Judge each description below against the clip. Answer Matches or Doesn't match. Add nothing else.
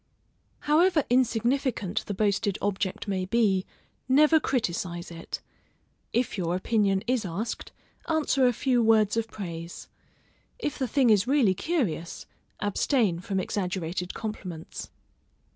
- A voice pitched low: Doesn't match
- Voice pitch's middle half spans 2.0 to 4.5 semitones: Doesn't match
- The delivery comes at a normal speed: Doesn't match